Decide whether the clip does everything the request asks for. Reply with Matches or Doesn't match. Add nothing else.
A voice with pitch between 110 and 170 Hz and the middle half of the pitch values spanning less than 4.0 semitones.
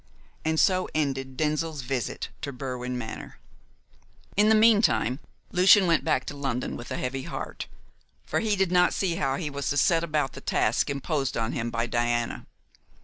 Doesn't match